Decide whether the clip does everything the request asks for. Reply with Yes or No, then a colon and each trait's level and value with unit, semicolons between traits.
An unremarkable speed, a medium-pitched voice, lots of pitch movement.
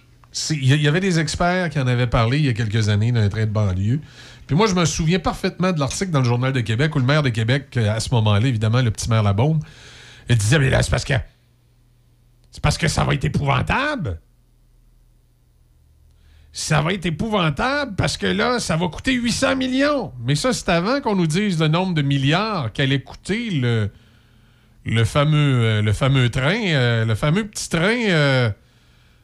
No: average, 195 wpm; low, 130 Hz; wide, 7.1 semitones